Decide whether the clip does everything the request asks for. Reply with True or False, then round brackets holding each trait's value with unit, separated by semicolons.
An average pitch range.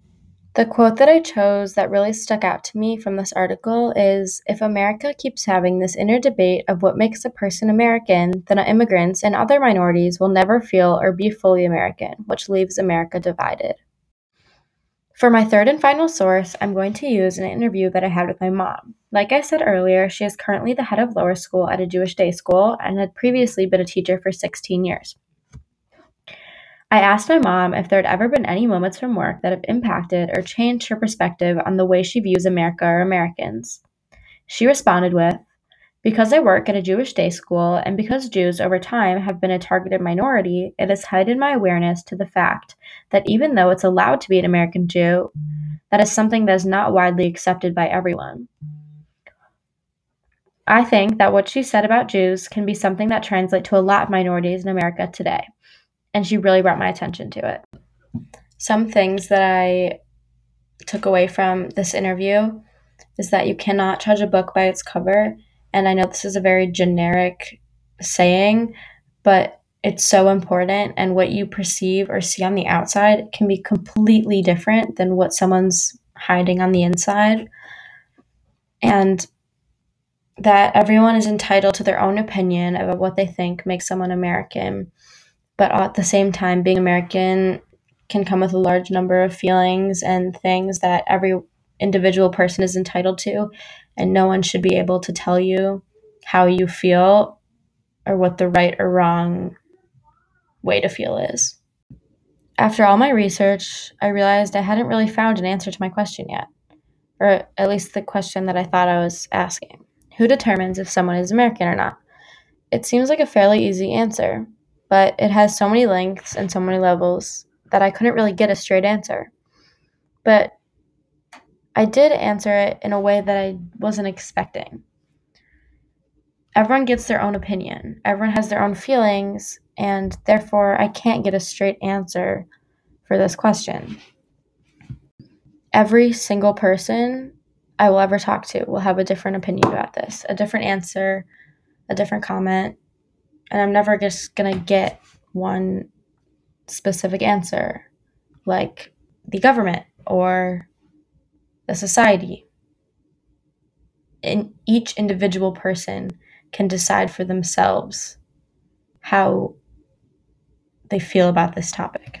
False (2.3 semitones)